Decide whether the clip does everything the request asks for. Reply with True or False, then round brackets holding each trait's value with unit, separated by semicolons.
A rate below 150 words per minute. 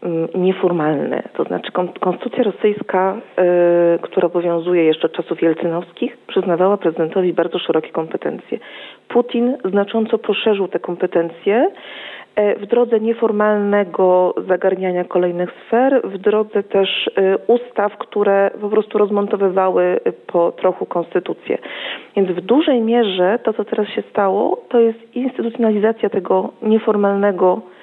True (110 wpm)